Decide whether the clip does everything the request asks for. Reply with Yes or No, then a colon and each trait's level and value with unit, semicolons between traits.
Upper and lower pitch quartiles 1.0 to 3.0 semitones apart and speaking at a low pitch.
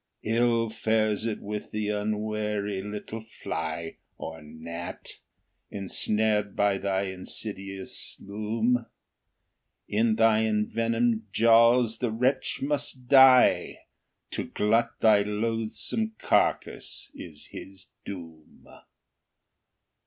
Yes: narrow, 2.4 semitones; low, 110 Hz